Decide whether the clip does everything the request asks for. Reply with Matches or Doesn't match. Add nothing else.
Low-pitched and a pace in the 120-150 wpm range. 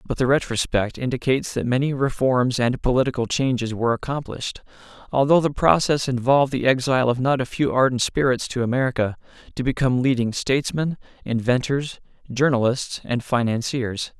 Matches